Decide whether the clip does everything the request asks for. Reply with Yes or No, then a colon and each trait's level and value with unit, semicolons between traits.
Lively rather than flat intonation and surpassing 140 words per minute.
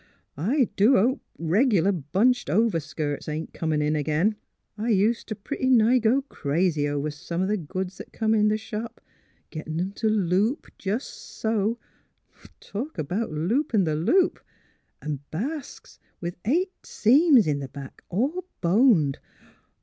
Yes: wide, 6.7 semitones; average, 150 wpm